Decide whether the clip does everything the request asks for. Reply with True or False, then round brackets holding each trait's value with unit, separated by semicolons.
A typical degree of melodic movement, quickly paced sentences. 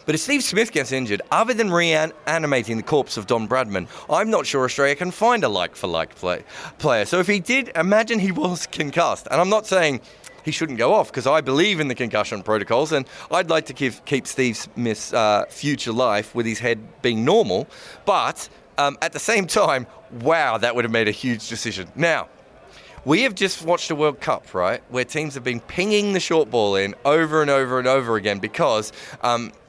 False (6.6 semitones; 210 wpm)